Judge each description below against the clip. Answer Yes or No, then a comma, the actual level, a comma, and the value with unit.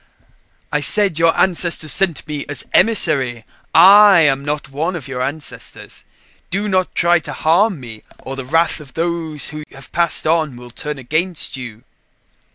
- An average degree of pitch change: Yes, average, 4.2 semitones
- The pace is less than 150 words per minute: No, average, 165 wpm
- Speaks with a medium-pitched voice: Yes, medium, 155 Hz